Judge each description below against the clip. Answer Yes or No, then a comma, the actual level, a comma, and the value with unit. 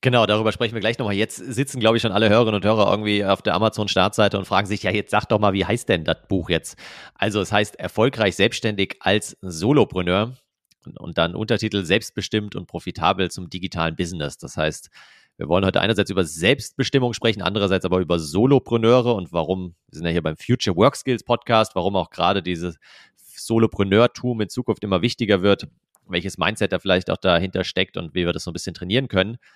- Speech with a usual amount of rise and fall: Yes, average, 3.5 semitones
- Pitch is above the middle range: No, low, 105 Hz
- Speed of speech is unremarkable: No, fast, 205 wpm